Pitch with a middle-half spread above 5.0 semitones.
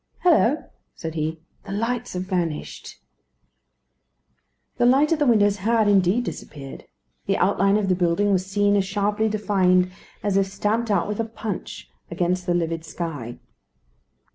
No: average, 3.4 semitones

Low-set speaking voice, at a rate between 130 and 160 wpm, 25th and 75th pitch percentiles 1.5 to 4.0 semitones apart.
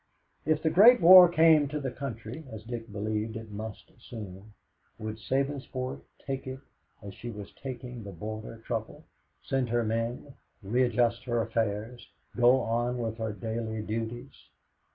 Yes: low, 115 Hz; average, 150 wpm; average, 3.3 semitones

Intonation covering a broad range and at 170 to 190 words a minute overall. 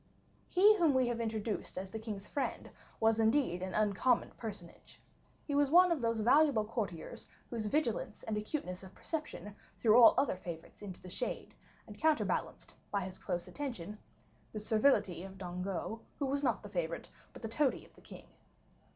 Yes: wide, 5.7 semitones; average, 175 wpm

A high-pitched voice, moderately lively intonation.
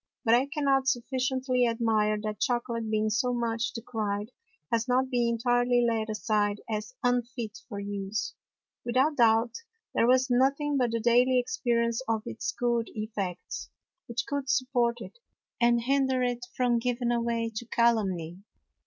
No: high, 235 Hz; narrow, 2.3 semitones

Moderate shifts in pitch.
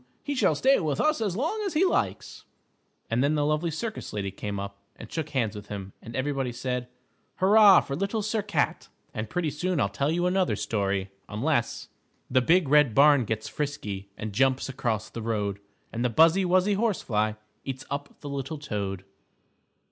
No: wide, 8.7 semitones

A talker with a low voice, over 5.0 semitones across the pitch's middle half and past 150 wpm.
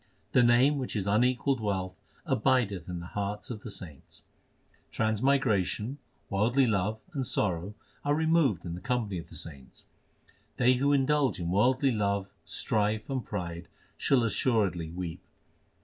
No: low, 110 Hz; wide, 5.6 semitones; average, 145 wpm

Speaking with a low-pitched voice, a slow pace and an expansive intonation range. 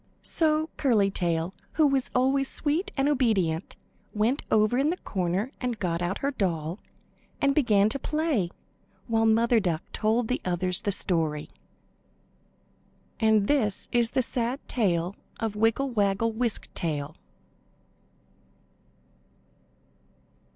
No: high, 220 Hz; slow, 125 wpm; wide, 6.0 semitones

